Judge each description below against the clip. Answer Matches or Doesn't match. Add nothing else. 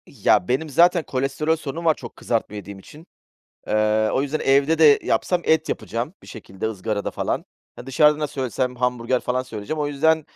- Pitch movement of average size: Matches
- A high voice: Doesn't match